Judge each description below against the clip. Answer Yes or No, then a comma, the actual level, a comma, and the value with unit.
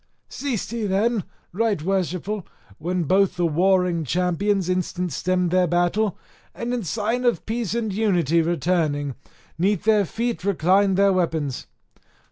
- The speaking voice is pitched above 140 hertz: Yes, medium, 185 Hz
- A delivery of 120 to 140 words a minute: Yes, slow, 135 wpm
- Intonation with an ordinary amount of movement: Yes, average, 3.3 semitones